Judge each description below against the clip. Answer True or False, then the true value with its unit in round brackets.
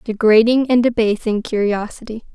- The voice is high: True (225 Hz)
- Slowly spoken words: True (100 wpm)